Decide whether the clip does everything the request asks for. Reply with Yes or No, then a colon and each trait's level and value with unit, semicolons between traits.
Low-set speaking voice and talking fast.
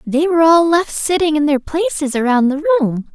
No: very high, 290 Hz; fast, 210 wpm